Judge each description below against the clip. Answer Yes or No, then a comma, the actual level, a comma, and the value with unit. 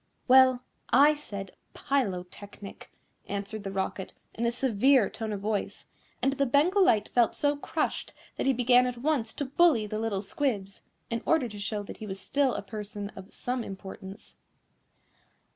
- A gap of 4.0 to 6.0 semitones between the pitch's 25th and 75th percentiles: Yes, average, 4.8 semitones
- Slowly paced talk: No, average, 165 wpm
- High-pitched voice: Yes, high, 225 Hz